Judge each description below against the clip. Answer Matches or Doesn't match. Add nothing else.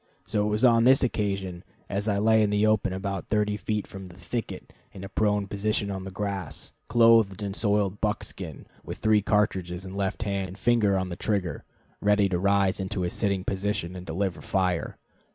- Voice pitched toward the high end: Doesn't match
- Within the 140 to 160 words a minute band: Doesn't match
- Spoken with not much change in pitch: Matches